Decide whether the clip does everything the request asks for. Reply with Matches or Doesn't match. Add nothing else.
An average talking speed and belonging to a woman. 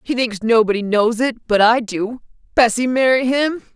Matches